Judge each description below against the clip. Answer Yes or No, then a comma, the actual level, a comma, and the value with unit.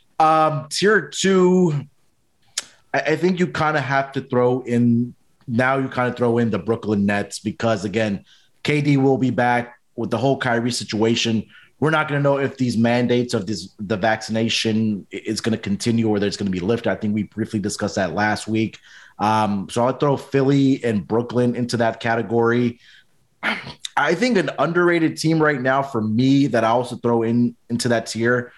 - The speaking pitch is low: Yes, low, 120 Hz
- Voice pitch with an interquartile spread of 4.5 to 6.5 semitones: No, average, 3.6 semitones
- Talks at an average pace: Yes, average, 185 wpm